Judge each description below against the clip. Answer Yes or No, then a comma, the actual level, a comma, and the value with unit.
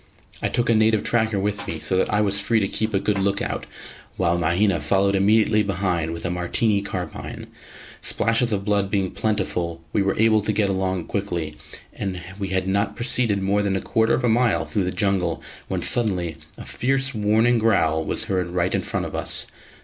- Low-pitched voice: Yes, low, 100 Hz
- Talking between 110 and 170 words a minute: No, fast, 205 wpm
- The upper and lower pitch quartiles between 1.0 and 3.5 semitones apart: Yes, average, 2.8 semitones